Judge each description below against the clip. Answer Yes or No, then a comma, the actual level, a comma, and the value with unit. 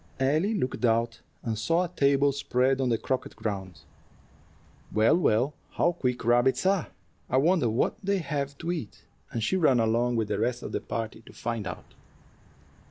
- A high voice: No, low, 125 Hz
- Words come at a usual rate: Yes, average, 175 wpm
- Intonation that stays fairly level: No, average, 4.8 semitones